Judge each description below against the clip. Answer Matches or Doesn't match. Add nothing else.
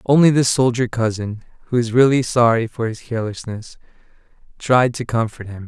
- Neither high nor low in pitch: Doesn't match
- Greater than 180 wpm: Doesn't match